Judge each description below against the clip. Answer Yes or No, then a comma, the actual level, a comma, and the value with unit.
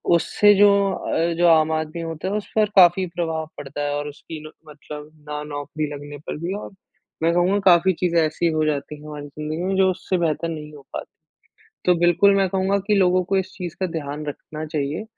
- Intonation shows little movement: No, average, 3.4 semitones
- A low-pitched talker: No, medium, 165 Hz